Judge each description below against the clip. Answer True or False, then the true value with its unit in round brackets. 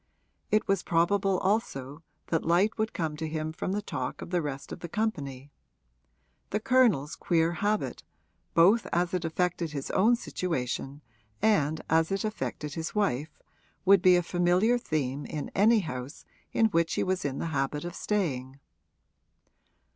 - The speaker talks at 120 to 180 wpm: True (160 wpm)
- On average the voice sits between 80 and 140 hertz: False (170 Hz)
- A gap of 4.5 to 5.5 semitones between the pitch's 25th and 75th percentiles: True (5.0 semitones)